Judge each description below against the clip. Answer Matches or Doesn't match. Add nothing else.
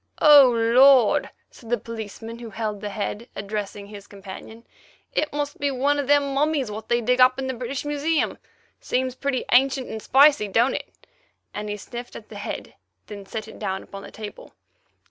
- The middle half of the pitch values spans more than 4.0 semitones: Matches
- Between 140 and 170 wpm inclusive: Doesn't match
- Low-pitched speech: Doesn't match